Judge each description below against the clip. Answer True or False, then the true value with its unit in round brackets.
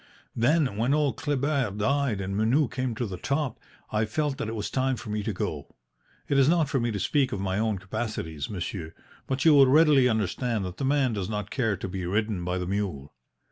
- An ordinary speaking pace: False (220 wpm)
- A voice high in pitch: False (110 Hz)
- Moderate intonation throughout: False (5.7 semitones)